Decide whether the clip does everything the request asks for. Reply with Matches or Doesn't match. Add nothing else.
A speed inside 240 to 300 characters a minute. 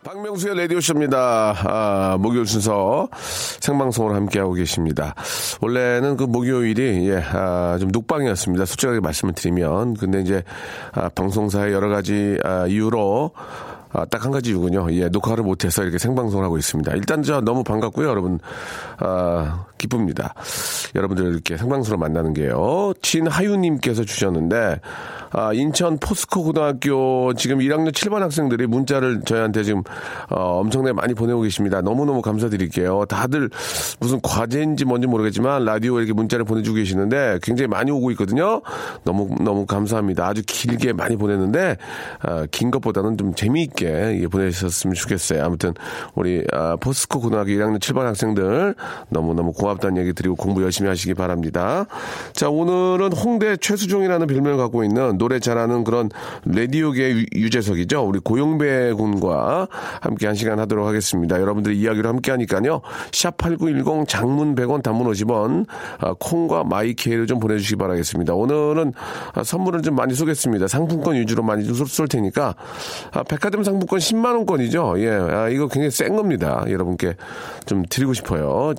Doesn't match